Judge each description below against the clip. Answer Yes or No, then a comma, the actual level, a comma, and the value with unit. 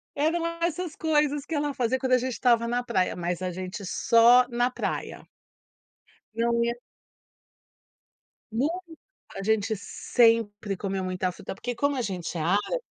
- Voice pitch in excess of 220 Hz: Yes, high, 235 Hz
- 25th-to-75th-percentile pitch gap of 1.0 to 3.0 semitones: No, average, 4.9 semitones